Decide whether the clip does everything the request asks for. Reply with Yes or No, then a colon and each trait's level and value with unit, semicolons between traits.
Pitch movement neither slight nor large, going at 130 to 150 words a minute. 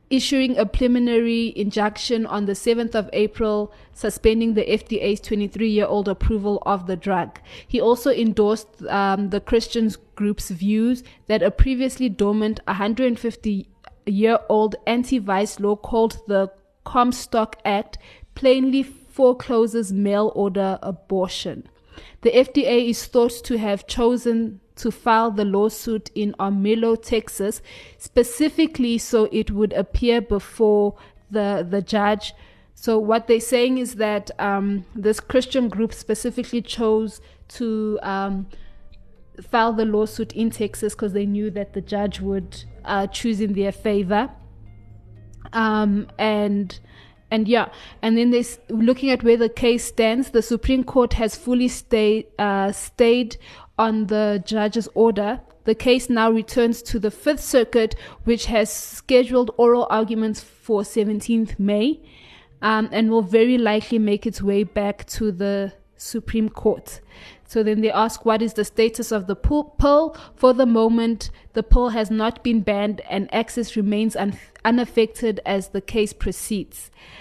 No: narrow, 2.3 semitones; average, 140 wpm